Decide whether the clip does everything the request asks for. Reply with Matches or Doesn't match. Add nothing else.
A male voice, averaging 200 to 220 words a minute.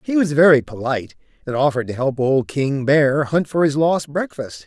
Matches